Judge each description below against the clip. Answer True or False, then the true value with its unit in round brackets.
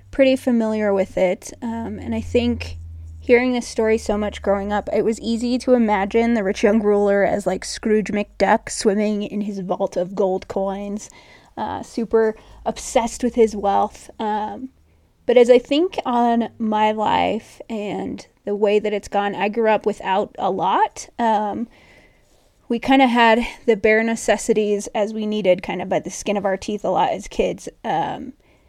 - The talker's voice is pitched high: True (215 Hz)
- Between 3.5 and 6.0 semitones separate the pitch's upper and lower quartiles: False (2.5 semitones)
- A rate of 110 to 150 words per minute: False (180 wpm)